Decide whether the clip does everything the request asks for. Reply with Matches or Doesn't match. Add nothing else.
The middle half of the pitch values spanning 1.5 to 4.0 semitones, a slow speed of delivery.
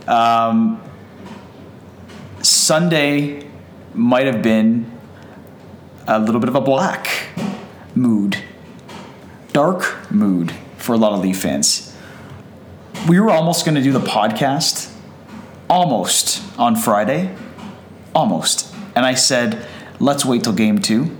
Doesn't match